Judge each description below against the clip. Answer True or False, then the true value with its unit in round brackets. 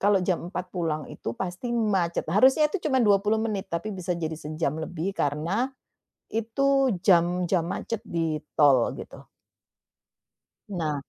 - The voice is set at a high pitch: False (180 Hz)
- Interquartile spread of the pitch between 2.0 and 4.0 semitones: False (4.5 semitones)